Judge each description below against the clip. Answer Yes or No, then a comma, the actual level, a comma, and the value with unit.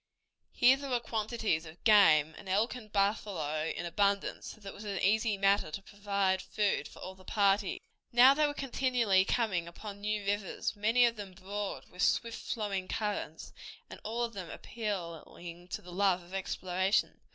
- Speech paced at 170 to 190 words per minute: Yes, average, 180 wpm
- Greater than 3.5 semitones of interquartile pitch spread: No, average, 2.8 semitones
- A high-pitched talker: Yes, high, 200 Hz